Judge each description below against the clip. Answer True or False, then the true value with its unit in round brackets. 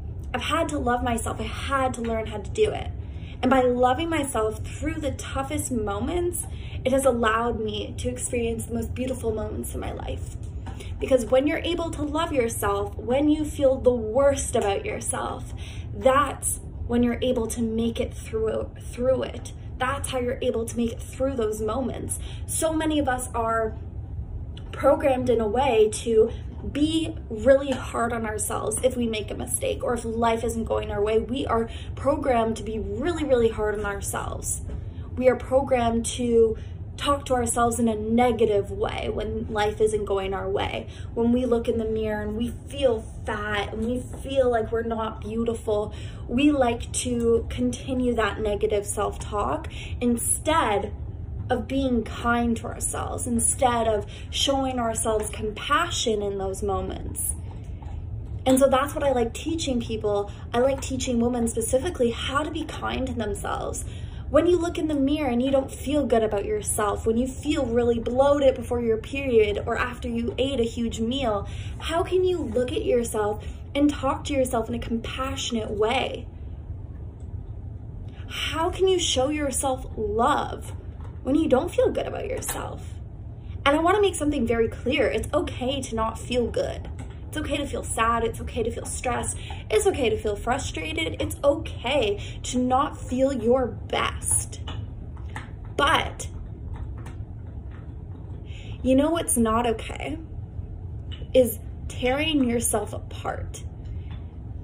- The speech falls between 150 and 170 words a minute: True (160 wpm)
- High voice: True (235 Hz)